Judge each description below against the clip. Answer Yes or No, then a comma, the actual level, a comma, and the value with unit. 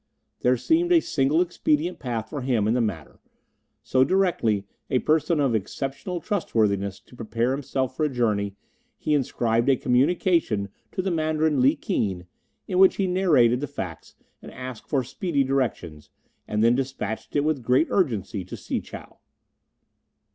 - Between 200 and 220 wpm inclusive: No, average, 160 wpm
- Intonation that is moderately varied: No, wide, 5.7 semitones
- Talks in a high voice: No, low, 130 Hz